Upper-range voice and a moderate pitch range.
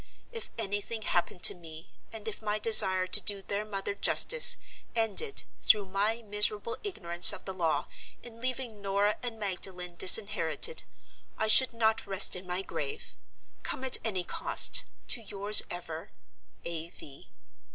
Yes: high, 205 Hz; average, 3.5 semitones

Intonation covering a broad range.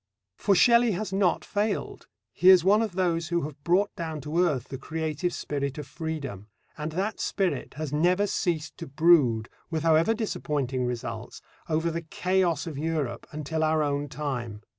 No: average, 3.9 semitones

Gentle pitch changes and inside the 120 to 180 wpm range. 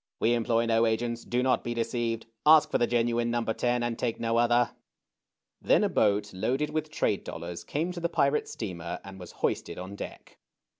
No: narrow, 1.8 semitones; average, 195 wpm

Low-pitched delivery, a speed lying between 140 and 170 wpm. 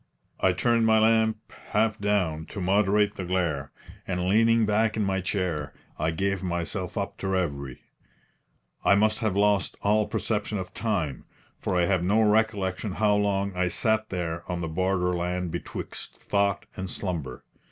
Yes: very low, 95 Hz; average, 160 wpm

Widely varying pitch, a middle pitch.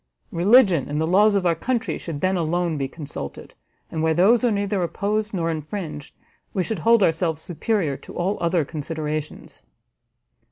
No: average, 4.4 semitones; medium, 175 Hz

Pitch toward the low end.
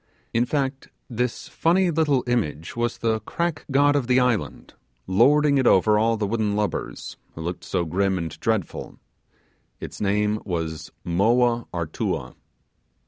Yes: low, 115 Hz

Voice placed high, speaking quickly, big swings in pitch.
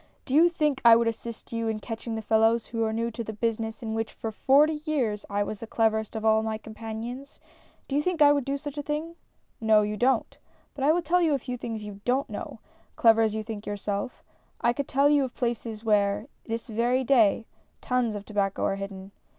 No: high, 230 Hz; fast, 225 wpm; average, 3.6 semitones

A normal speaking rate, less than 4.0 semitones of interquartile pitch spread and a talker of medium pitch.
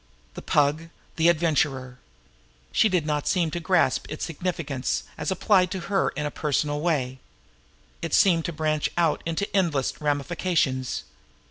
Yes: average, 150 wpm; average, 2.9 semitones; medium, 155 Hz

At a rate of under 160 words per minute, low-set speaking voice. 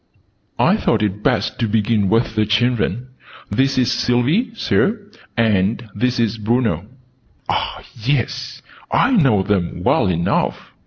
Yes: slow, 135 wpm; low, 115 Hz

